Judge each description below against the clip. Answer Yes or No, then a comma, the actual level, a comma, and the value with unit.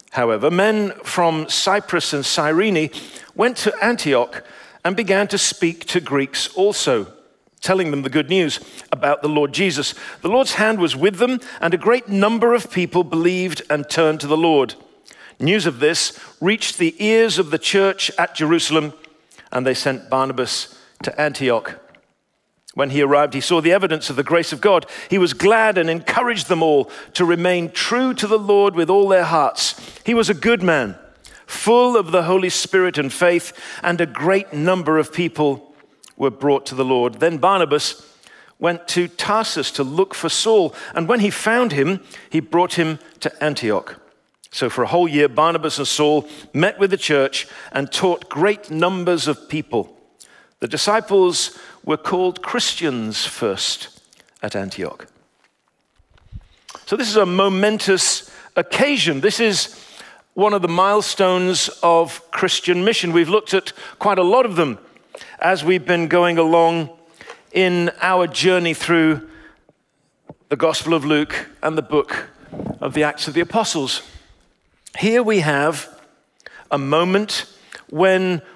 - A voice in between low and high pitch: Yes, medium, 175 Hz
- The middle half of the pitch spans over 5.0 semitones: No, average, 4.3 semitones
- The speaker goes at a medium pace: Yes, average, 160 wpm